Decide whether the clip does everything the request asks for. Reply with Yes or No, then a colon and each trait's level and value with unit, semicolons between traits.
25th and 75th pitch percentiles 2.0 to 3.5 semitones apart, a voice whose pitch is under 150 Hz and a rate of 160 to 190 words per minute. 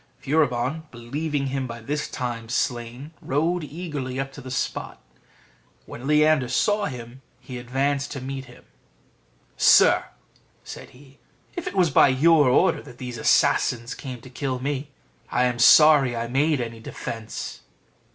No: average, 3.2 semitones; low, 135 Hz; average, 150 wpm